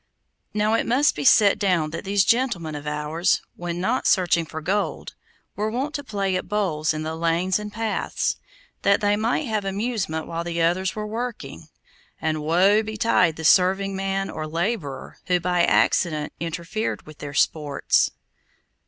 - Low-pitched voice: No, medium, 185 Hz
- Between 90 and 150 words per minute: No, average, 165 wpm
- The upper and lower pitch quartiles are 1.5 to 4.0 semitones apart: No, average, 4.6 semitones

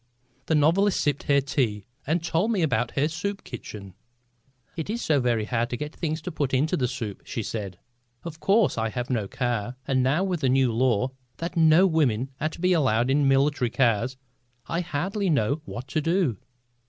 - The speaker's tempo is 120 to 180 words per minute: No, average, 195 wpm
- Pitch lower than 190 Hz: Yes, medium, 140 Hz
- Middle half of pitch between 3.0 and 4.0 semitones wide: No, average, 5.2 semitones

